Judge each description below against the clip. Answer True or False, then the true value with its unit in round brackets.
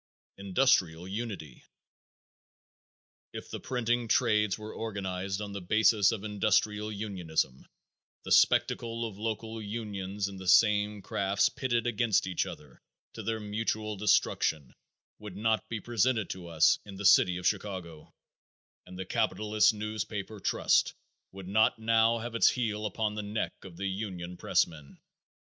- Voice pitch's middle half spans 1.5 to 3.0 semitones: True (2.6 semitones)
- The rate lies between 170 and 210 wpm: False (140 wpm)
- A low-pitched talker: True (105 Hz)